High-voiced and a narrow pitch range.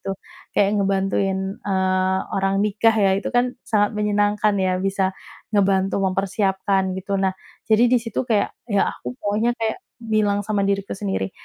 Yes: high, 200 Hz; narrow, 1.6 semitones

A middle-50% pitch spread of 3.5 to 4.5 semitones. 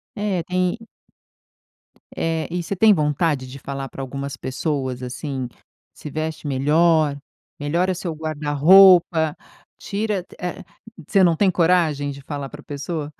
Yes: average, 4.0 semitones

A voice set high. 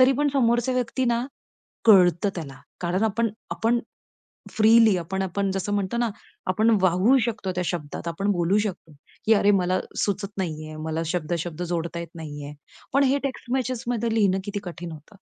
Yes: high, 195 Hz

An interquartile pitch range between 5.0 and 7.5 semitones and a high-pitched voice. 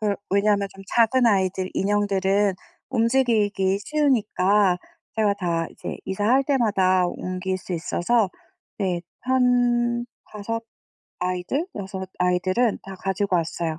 No: average, 3.7 semitones; high, 200 Hz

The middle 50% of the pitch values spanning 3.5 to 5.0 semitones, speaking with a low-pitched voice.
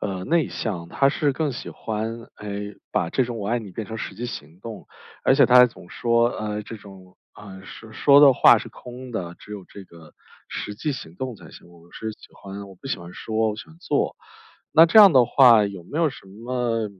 Yes: average, 4.2 semitones; low, 110 Hz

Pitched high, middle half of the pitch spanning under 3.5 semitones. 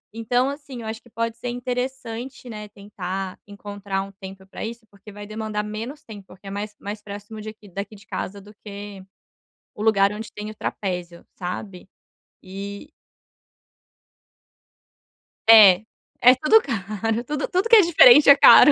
Yes: high, 210 Hz; average, 2.9 semitones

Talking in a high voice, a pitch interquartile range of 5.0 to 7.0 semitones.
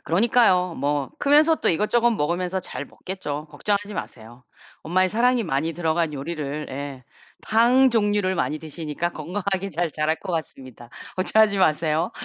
No: medium, 175 Hz; average, 5.3 semitones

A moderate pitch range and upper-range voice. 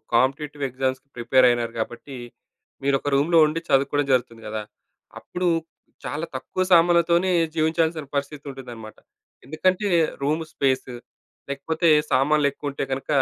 No: average, 3.4 semitones; medium, 140 Hz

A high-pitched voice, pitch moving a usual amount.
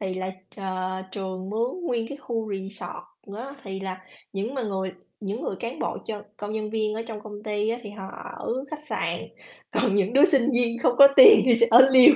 Yes: high, 215 Hz; average, 3.8 semitones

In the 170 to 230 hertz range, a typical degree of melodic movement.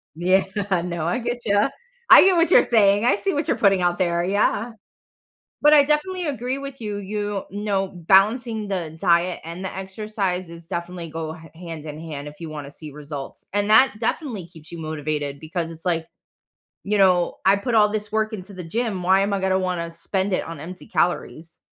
Yes: high, 190 Hz; average, 4.1 semitones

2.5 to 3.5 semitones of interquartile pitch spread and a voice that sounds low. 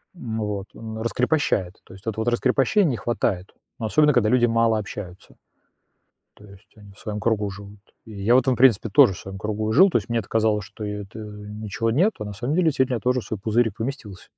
Yes: average, 2.9 semitones; low, 110 Hz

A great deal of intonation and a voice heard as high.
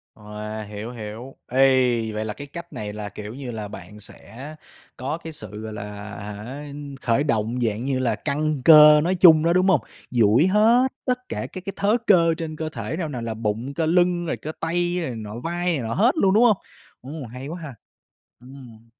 No: wide, 7.3 semitones; low, 135 Hz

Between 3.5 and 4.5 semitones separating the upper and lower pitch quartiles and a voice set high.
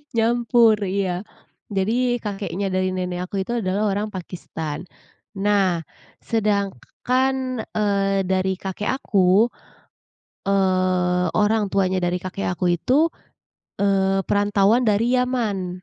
No: average, 2.8 semitones; high, 200 Hz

